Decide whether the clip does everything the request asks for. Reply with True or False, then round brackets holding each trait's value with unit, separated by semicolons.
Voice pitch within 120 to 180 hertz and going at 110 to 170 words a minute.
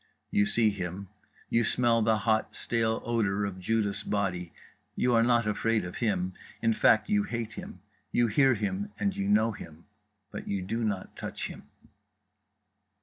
False (110 Hz; 165 wpm)